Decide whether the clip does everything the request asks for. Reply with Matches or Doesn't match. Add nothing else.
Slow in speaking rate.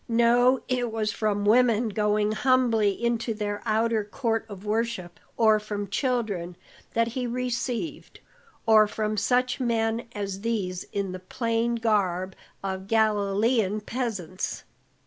Matches